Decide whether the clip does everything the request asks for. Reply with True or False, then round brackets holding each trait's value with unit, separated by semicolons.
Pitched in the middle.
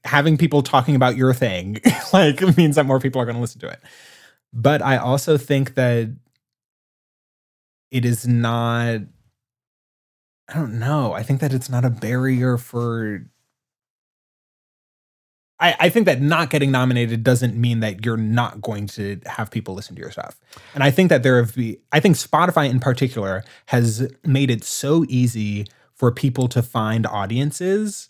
False (125 Hz)